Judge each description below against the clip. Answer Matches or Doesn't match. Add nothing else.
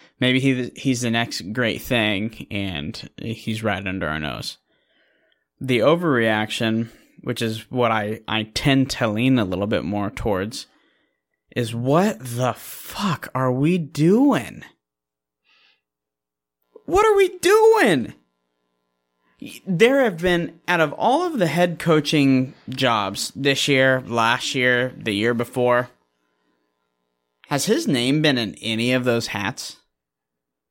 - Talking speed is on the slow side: Matches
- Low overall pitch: Matches